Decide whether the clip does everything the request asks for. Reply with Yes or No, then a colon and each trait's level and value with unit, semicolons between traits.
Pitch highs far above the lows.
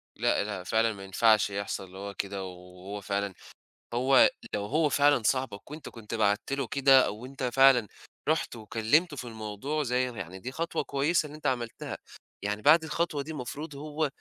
Yes: wide, 5.9 semitones